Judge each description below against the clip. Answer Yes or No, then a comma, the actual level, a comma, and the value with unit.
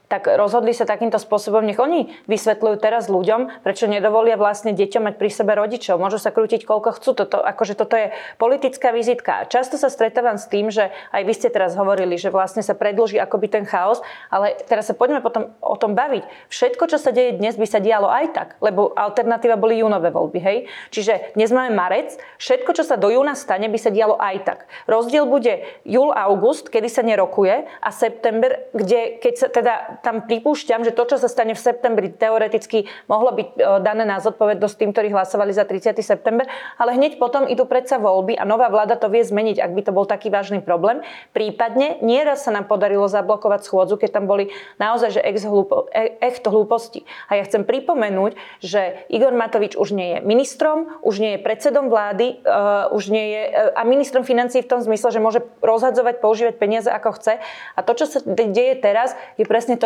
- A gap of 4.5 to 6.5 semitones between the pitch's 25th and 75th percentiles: No, average, 2.8 semitones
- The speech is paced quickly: Yes, fast, 195 wpm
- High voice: Yes, high, 225 Hz